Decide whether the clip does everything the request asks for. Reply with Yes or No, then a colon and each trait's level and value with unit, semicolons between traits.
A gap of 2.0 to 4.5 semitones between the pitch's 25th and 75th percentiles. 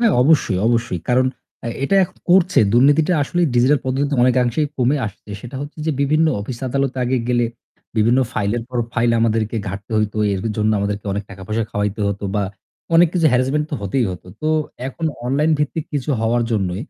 No: average, 5.2 semitones